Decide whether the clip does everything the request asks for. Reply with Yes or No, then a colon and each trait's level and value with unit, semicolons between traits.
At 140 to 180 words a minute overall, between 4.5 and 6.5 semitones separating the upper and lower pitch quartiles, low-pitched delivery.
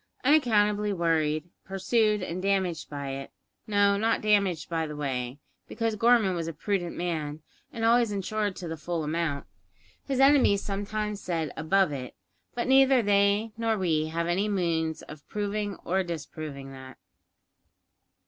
No: average, 150 wpm; average, 4.8 semitones; high, 190 Hz